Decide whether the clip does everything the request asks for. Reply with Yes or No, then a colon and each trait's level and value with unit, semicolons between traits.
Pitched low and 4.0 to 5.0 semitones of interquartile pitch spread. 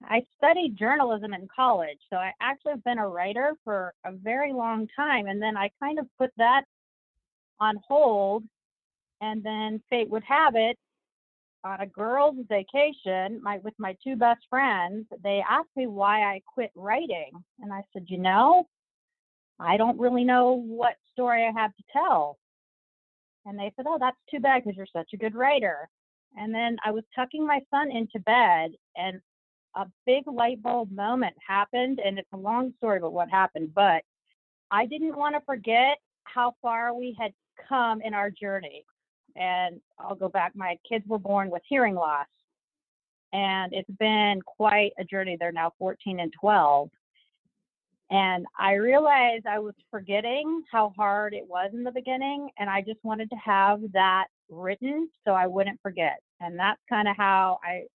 No: high, 215 Hz; average, 4.4 semitones